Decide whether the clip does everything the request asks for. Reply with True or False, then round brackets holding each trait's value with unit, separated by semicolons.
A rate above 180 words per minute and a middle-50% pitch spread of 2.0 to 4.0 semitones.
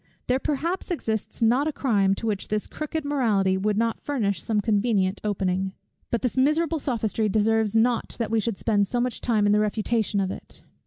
True (195 wpm; 3.5 semitones)